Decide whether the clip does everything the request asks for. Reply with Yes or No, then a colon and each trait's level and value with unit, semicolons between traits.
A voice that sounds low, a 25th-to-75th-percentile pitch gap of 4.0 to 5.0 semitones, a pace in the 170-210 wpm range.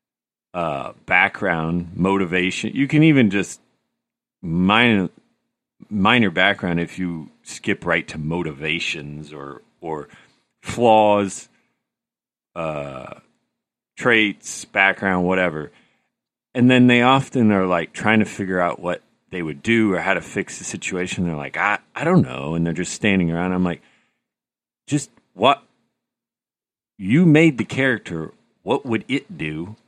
No: very low, 90 Hz; average, 4.7 semitones; slow, 135 wpm